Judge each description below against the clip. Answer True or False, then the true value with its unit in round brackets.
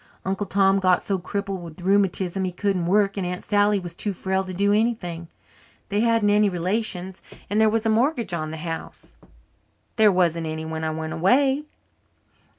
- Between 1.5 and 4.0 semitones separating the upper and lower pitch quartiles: True (3.0 semitones)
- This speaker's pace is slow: False (180 wpm)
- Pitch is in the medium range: False (195 Hz)